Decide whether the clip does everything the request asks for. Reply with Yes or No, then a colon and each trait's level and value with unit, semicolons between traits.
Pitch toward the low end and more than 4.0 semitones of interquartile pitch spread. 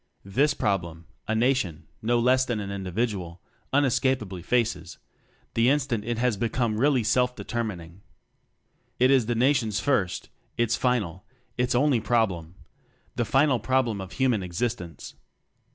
Yes: low, 115 Hz; average, 4.5 semitones